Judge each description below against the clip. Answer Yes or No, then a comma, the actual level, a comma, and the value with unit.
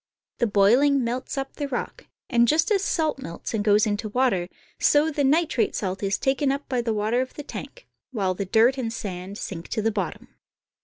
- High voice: Yes, high, 235 Hz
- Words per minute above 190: Yes, fast, 205 wpm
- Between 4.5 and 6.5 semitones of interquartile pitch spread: Yes, average, 5.1 semitones